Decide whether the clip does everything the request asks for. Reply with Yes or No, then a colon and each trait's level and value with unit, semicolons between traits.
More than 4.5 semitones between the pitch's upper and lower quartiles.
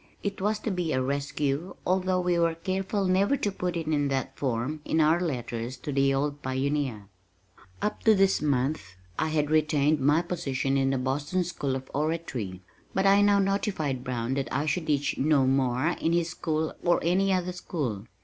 Yes: average, 4.9 semitones